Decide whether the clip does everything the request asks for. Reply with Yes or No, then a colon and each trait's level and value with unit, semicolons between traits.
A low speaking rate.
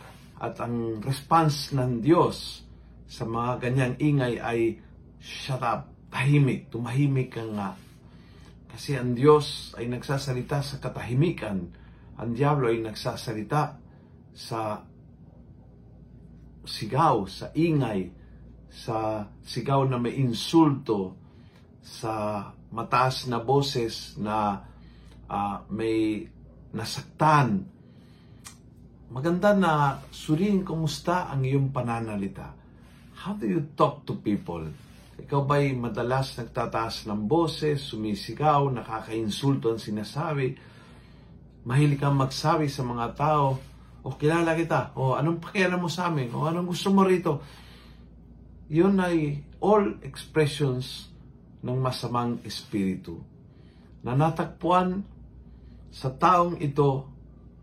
Yes: slow, 105 wpm